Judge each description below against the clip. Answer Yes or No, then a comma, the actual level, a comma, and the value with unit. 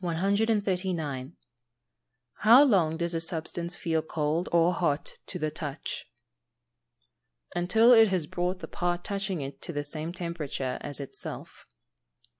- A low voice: No, medium, 170 Hz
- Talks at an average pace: No, slow, 130 wpm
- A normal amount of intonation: Yes, average, 3.2 semitones